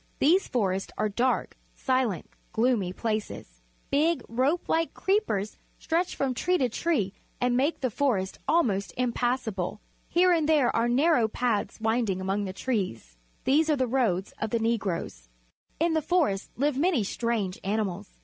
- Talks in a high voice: Yes, high, 240 Hz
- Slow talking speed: No, average, 150 wpm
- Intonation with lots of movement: Yes, wide, 6.2 semitones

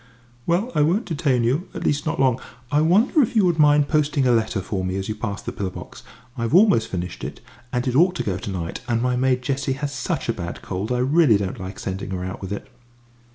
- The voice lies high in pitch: No, low, 125 Hz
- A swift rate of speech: Yes, fast, 245 wpm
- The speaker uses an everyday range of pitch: No, wide, 7.4 semitones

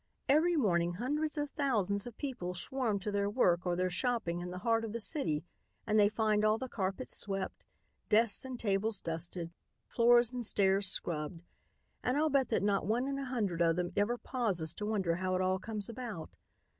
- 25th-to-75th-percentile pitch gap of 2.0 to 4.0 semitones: No, average, 5.0 semitones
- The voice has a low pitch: No, high, 210 Hz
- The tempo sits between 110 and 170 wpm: No, average, 195 wpm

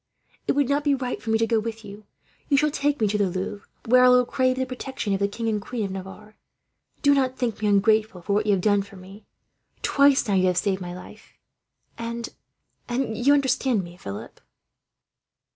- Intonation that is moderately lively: Yes, average, 4.4 semitones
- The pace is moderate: No, fast, 215 wpm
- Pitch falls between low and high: No, high, 220 Hz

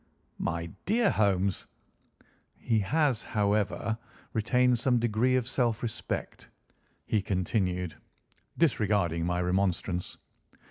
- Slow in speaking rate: Yes, slow, 95 wpm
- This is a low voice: Yes, low, 105 Hz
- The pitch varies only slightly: No, average, 4.7 semitones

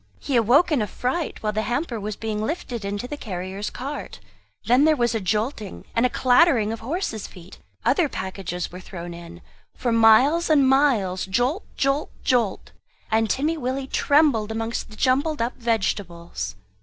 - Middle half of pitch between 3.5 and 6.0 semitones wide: Yes, average, 5.1 semitones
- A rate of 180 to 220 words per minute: No, average, 170 wpm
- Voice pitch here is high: Yes, high, 230 Hz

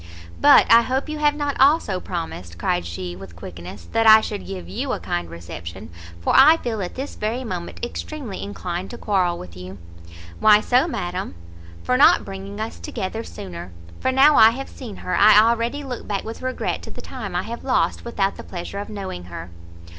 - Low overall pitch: No, high, 205 Hz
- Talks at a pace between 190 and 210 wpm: Yes, average, 200 wpm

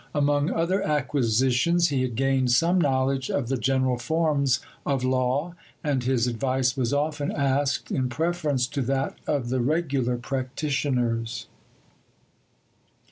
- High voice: No, low, 135 Hz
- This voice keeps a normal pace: No, slow, 130 wpm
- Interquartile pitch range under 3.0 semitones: Yes, narrow, 2.6 semitones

